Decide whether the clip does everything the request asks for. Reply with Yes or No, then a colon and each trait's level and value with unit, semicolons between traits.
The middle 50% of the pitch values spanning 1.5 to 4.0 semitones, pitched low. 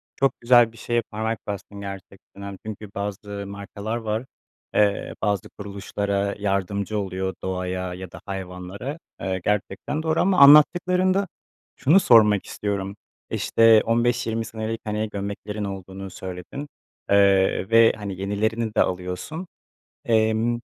Yes: average, 2.8 semitones; low, 105 Hz